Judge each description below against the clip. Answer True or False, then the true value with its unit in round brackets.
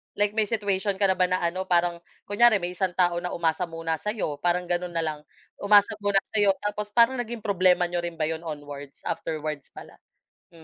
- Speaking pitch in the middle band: True (180 Hz)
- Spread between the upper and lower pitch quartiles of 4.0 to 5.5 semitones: False (3.6 semitones)